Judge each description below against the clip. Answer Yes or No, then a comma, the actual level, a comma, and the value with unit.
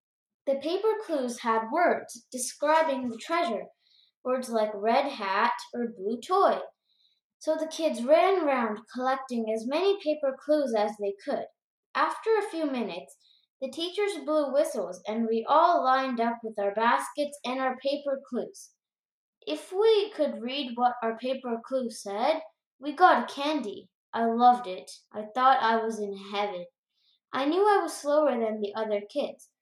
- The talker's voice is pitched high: Yes, very high, 260 Hz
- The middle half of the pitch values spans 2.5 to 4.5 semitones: No, average, 5.3 semitones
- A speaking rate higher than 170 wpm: No, average, 160 wpm